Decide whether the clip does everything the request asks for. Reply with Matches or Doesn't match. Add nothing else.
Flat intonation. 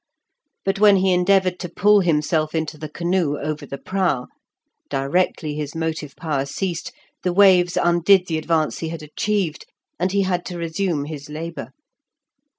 Doesn't match